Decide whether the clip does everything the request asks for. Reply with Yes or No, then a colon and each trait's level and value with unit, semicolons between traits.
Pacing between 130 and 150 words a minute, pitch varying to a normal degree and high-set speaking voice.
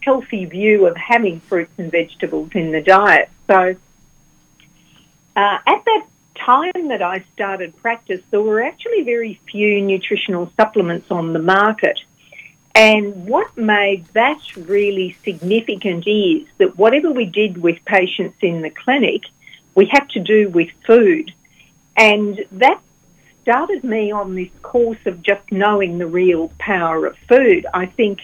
Yes: average, 145 wpm; average, 3.9 semitones; high, 200 Hz